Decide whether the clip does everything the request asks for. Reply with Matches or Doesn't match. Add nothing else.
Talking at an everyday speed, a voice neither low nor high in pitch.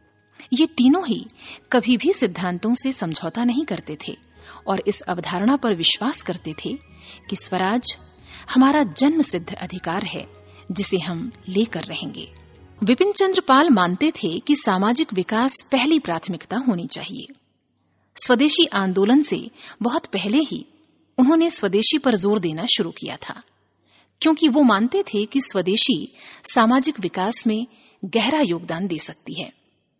Doesn't match